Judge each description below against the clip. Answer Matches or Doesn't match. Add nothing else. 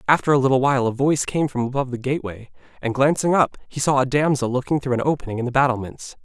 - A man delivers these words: Matches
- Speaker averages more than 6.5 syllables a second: Matches